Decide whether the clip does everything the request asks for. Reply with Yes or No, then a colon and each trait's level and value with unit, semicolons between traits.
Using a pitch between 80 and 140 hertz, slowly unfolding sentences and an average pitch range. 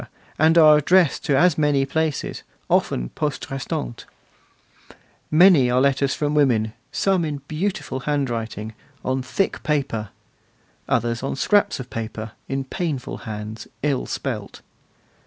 Yes: low, 135 Hz; slow, 125 wpm; average, 4.4 semitones